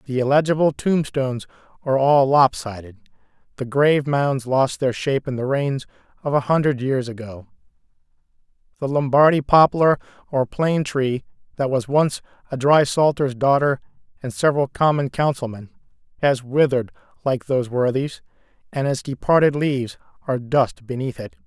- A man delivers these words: Yes, male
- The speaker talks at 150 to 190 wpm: No, average, 140 wpm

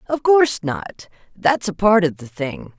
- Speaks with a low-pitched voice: No, high, 195 Hz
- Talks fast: No, average, 195 wpm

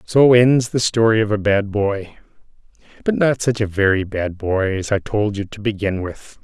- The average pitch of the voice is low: Yes, low, 105 Hz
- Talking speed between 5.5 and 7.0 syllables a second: No, 4.6 syllables/s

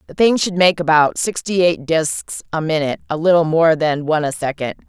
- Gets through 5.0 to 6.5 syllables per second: Yes, 5.4 syllables/s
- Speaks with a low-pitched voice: No, medium, 160 Hz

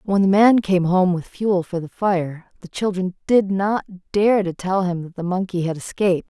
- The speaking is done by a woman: Yes, female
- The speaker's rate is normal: No, fast, 215 wpm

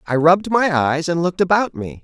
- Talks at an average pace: No, fast, 235 wpm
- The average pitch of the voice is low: No, medium, 165 Hz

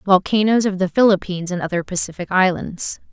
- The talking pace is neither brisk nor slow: Yes, average, 155 wpm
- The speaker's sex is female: Yes, female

